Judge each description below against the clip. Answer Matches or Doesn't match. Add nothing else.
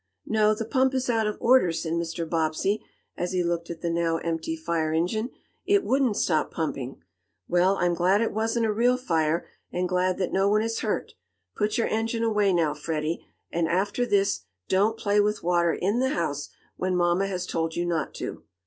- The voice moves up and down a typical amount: Matches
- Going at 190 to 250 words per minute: Matches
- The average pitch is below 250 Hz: Matches